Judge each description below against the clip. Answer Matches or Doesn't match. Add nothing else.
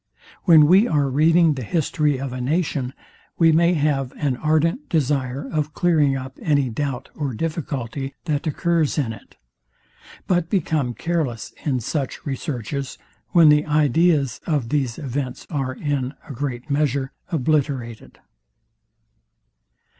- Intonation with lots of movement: Doesn't match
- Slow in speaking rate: Matches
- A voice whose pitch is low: Doesn't match